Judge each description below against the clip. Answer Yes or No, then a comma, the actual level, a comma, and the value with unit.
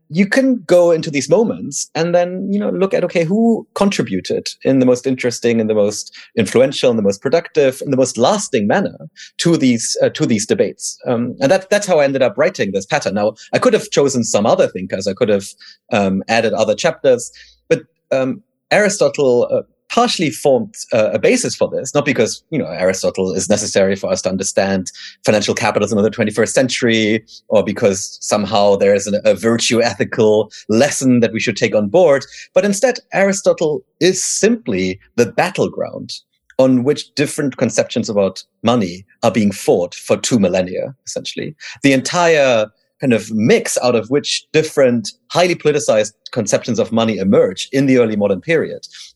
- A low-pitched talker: No, medium, 145 Hz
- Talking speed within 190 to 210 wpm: No, average, 180 wpm